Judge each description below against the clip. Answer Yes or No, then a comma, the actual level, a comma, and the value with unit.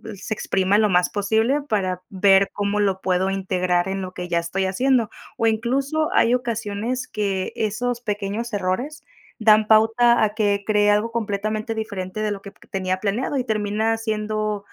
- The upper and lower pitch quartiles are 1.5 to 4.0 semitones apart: Yes, narrow, 2.6 semitones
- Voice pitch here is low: No, high, 210 Hz